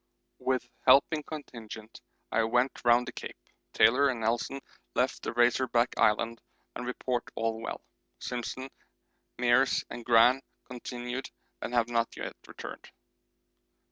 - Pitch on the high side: No, low, 120 Hz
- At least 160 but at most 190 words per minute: No, slow, 135 wpm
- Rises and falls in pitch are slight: Yes, narrow, 1.7 semitones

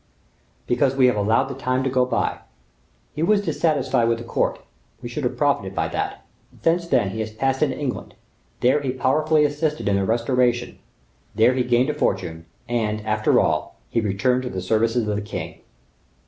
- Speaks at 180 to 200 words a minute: Yes, average, 190 wpm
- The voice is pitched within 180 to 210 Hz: No, low, 125 Hz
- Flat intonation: No, average, 3.6 semitones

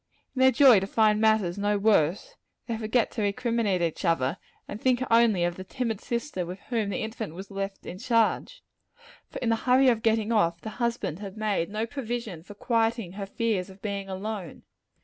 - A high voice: Yes, high, 215 Hz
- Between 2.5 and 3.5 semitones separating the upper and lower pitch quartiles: Yes, average, 3.1 semitones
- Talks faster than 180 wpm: Yes, average, 195 wpm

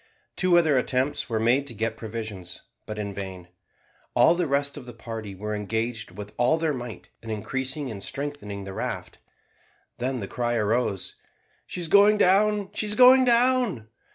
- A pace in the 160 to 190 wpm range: Yes, average, 175 wpm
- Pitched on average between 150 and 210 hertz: No, low, 120 Hz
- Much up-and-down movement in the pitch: Yes, wide, 7.2 semitones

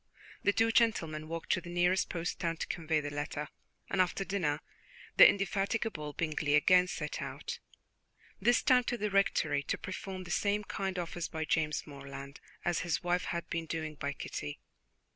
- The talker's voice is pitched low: No, medium, 170 Hz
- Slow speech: No, average, 175 wpm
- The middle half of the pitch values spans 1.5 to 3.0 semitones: No, average, 4.0 semitones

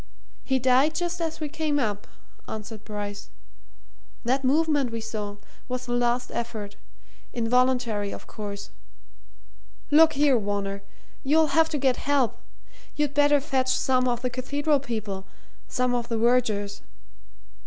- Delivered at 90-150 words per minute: Yes, slow, 135 wpm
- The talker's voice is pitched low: No, very high, 250 Hz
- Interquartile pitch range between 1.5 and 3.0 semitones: No, average, 4.8 semitones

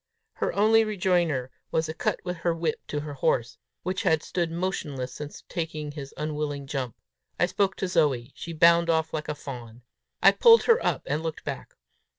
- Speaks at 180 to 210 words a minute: Yes, average, 185 wpm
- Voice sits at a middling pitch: Yes, medium, 160 Hz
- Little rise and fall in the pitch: No, average, 3.5 semitones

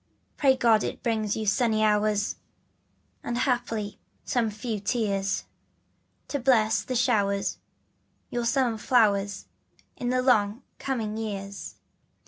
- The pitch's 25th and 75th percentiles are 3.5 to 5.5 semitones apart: No, average, 2.8 semitones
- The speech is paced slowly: Yes, slow, 115 wpm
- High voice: Yes, high, 220 Hz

